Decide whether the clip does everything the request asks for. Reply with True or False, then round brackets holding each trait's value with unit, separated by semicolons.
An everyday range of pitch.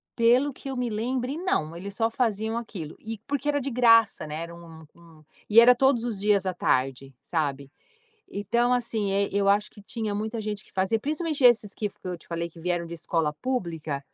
False (5.9 semitones)